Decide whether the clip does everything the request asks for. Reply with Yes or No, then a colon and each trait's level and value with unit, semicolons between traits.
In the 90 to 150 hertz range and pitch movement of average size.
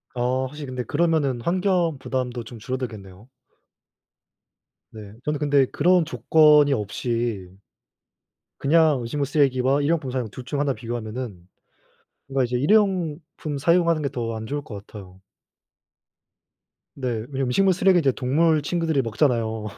Yes: low, 135 Hz; average, 4.5 semitones